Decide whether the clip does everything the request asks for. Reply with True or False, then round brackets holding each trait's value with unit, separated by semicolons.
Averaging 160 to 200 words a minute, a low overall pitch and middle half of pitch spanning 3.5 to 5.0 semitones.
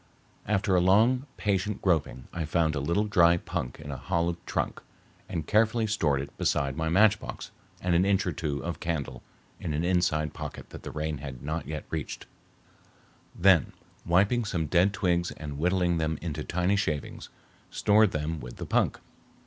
True (170 wpm; 85 Hz; 4.1 semitones)